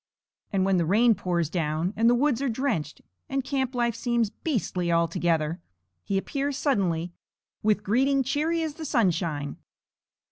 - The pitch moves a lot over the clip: Yes, wide, 7.5 semitones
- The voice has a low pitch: No, high, 215 Hz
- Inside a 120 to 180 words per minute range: Yes, average, 150 wpm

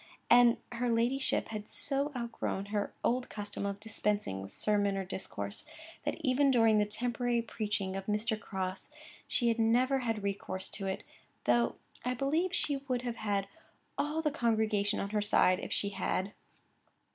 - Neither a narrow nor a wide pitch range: Yes, average, 3.6 semitones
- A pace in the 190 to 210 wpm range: No, average, 165 wpm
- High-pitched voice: Yes, high, 220 Hz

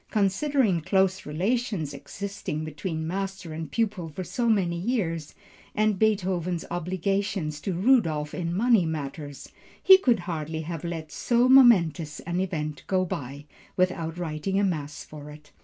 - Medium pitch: Yes, medium, 175 Hz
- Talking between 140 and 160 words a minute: Yes, average, 145 wpm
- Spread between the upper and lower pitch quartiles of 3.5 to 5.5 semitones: Yes, average, 4.2 semitones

